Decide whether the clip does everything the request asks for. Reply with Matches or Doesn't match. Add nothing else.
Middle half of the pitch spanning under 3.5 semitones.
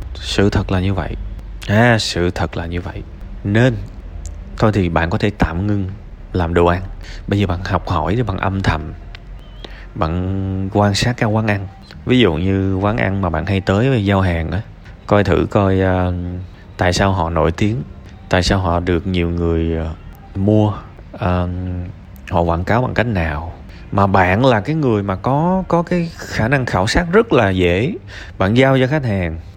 Matches